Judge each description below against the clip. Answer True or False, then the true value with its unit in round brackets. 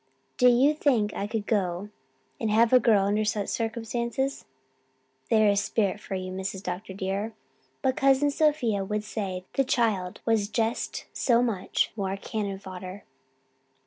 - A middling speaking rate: True (150 wpm)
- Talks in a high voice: True (215 Hz)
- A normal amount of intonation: True (3.4 semitones)